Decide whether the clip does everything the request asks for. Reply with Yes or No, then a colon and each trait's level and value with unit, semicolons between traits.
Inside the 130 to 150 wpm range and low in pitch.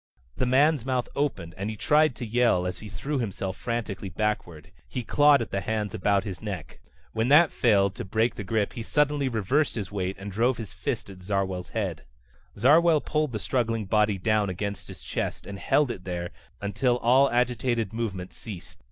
No: average, 190 wpm; low, 110 Hz